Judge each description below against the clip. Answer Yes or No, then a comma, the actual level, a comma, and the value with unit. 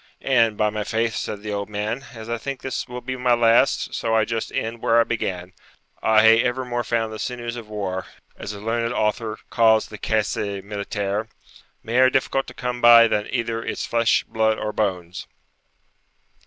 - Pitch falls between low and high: No, low, 115 Hz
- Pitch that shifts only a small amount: Yes, narrow, 2.0 semitones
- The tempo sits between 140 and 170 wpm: No, average, 185 wpm